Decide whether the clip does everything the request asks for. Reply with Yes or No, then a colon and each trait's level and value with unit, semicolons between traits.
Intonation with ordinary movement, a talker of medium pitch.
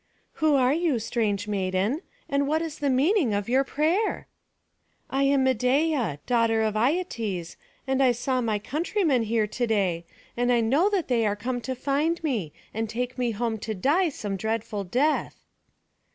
No: average, 4.7 semitones; high, 245 Hz